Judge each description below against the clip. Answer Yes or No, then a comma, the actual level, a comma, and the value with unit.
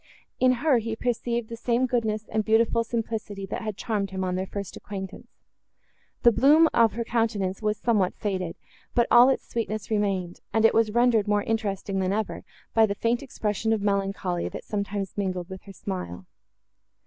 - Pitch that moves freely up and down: No, average, 2.9 semitones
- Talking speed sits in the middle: Yes, average, 180 wpm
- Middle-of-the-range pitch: No, high, 215 Hz